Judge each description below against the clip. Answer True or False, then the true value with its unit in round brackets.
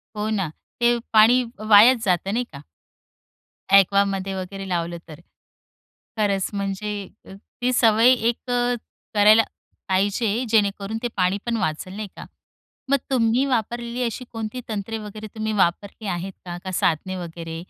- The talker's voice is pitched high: True (210 Hz)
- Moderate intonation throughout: True (3.1 semitones)